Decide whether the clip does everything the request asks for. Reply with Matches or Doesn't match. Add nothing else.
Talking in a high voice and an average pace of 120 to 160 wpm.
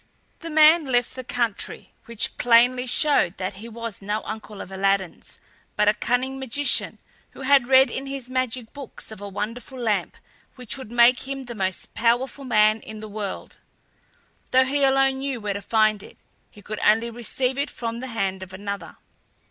Doesn't match